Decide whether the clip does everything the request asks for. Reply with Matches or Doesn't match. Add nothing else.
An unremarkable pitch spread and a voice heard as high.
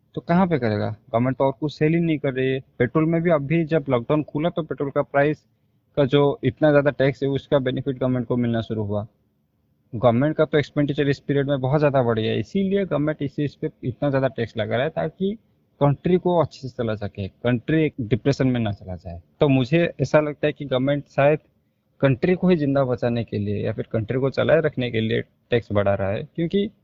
Doesn't match